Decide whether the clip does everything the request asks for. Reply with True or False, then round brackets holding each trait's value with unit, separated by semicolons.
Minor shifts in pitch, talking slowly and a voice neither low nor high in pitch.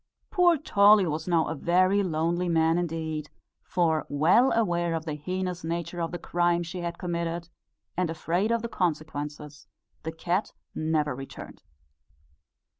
False (2.2 semitones; 145 wpm; 170 Hz)